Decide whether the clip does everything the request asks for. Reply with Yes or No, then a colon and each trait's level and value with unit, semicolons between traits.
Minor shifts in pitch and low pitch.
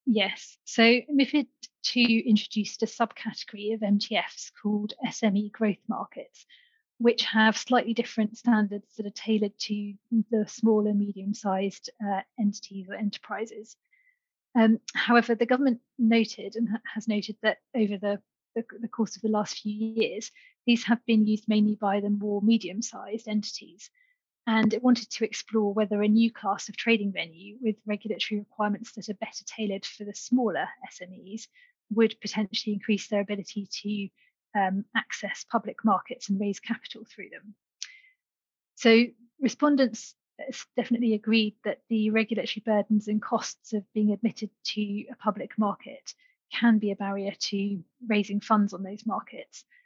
No: narrow, 2.2 semitones; high, 220 Hz